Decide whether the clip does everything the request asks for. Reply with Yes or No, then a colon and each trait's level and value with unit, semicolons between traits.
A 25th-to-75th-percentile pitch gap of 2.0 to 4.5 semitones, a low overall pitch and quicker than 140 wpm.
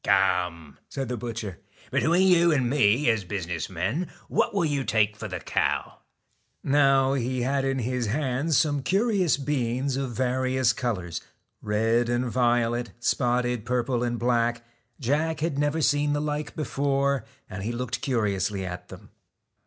Yes: average, 3.9 semitones; low, 125 Hz; average, 155 wpm